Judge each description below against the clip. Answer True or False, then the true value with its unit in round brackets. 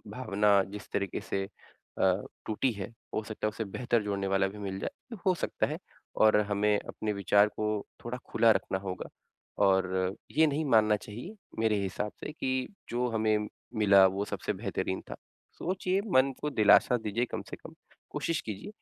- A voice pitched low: True (105 Hz)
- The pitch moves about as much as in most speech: True (3.3 semitones)